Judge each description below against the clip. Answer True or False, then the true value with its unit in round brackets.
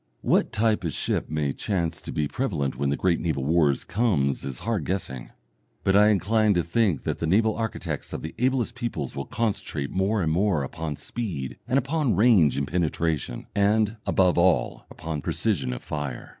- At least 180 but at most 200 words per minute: True (185 wpm)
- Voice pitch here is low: True (90 Hz)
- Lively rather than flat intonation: True (6.5 semitones)